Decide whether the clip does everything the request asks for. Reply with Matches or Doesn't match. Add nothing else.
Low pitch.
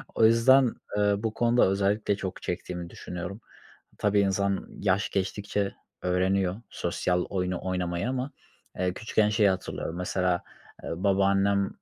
Matches